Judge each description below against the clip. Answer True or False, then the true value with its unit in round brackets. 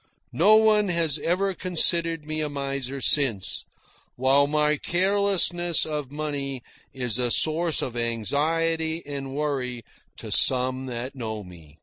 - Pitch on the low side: False (145 Hz)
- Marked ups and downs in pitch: False (4.3 semitones)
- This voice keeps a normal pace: False (130 wpm)